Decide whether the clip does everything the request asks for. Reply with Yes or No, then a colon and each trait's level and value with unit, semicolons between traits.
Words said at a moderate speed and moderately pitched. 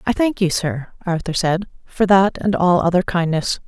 Yes: average, 195 wpm; medium, 180 Hz